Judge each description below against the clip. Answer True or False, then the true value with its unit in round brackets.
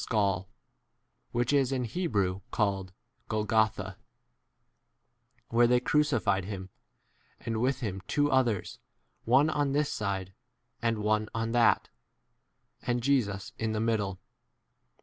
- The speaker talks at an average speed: False (120 wpm)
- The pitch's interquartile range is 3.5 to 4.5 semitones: True (3.9 semitones)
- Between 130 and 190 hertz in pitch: False (115 Hz)